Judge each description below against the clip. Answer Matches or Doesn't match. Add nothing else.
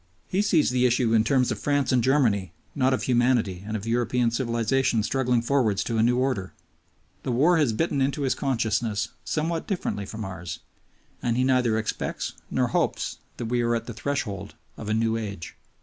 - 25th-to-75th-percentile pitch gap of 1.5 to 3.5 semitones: Matches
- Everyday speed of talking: Matches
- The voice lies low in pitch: Matches